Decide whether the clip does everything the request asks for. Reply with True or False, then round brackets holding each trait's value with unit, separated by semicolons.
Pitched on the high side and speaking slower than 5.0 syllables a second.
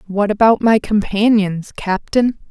True (210 Hz; 4.0 syllables/s)